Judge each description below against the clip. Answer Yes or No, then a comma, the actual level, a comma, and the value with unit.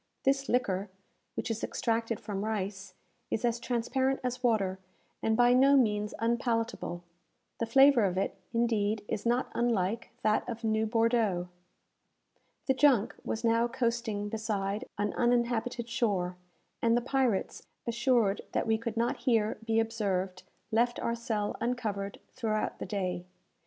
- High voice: Yes, high, 225 Hz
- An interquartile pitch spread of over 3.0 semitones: No, narrow, 2.6 semitones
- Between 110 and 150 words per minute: Yes, average, 140 wpm